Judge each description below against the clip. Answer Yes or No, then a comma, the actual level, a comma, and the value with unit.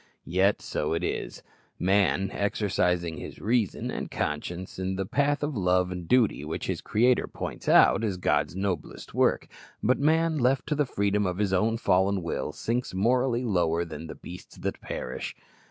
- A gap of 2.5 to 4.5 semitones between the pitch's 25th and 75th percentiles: No, average, 5.1 semitones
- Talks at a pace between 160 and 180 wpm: Yes, average, 170 wpm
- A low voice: Yes, very low, 95 Hz